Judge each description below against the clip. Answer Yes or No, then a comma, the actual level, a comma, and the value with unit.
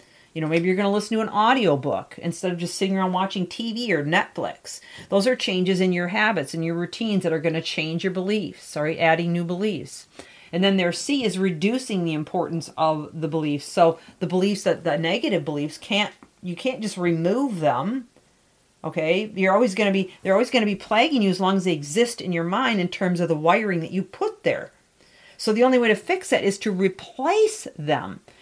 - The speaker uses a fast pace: Yes, fast, 220 wpm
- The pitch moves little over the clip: No, average, 4.0 semitones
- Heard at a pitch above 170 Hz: Yes, high, 190 Hz